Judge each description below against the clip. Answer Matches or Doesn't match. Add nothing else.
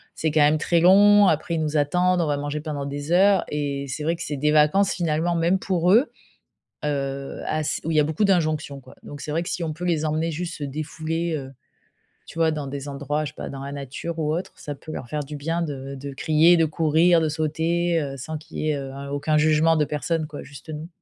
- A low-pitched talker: Doesn't match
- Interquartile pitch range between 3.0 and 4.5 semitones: Doesn't match